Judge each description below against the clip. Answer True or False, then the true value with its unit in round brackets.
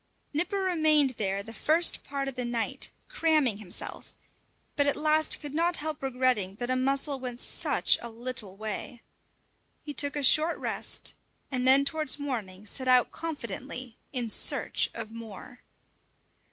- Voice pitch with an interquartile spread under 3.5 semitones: False (4.3 semitones)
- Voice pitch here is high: True (260 Hz)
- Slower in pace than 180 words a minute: True (155 wpm)